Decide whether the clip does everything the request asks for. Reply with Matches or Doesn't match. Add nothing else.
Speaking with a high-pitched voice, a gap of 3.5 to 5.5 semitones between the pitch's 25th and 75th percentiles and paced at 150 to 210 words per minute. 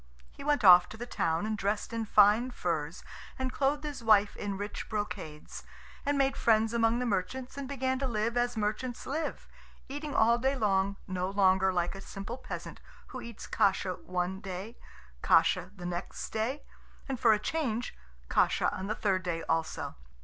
Matches